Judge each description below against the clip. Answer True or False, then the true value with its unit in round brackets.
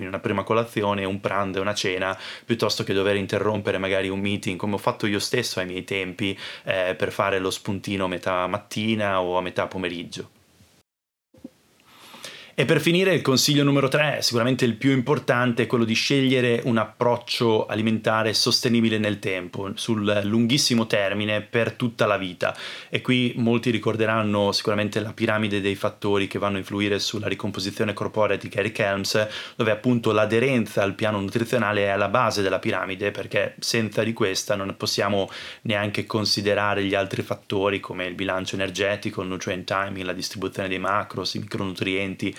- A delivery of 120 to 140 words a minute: False (165 wpm)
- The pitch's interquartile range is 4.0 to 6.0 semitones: False (2.9 semitones)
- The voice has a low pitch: True (105 Hz)